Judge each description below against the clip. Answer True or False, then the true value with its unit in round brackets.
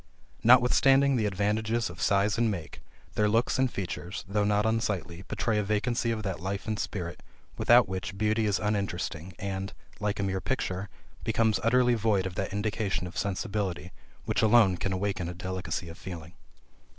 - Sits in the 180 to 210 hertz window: False (100 Hz)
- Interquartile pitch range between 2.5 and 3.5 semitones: True (2.9 semitones)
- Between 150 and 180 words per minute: True (170 wpm)